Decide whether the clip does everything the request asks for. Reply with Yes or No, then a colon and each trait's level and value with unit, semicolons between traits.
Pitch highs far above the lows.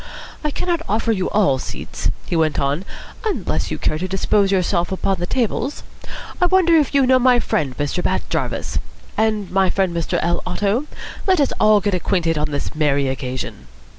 Yes: wide, 6.9 semitones